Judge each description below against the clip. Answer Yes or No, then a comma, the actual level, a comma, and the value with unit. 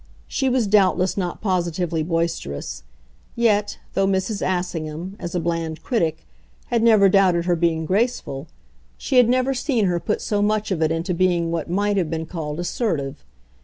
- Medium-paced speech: Yes, average, 165 wpm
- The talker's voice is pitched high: No, medium, 180 Hz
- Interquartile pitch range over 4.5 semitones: No, average, 3.8 semitones